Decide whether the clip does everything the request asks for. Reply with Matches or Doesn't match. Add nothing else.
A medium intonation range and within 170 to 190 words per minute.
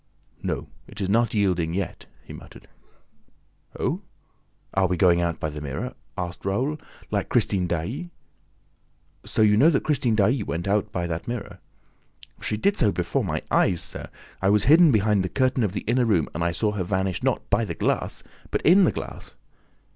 Matches